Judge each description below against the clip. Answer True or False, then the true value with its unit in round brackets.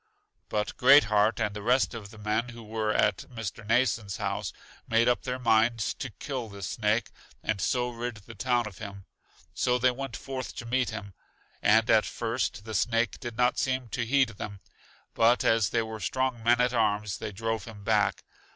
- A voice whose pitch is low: True (115 Hz)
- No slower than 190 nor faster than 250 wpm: True (195 wpm)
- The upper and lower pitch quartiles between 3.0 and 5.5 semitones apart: False (2.5 semitones)